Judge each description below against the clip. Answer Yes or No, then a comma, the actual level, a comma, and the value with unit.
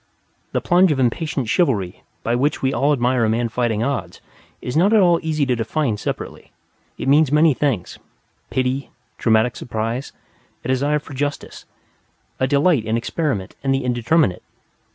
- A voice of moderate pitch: No, low, 130 Hz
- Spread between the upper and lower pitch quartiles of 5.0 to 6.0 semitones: No, average, 4.3 semitones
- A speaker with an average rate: Yes, average, 160 wpm